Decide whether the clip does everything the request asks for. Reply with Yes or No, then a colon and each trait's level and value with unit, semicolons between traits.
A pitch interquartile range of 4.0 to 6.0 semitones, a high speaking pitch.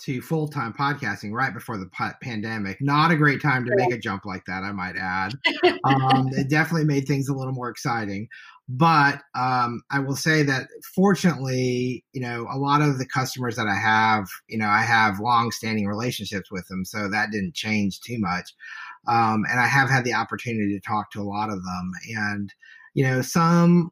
No: average, 5.2 semitones; low, 125 Hz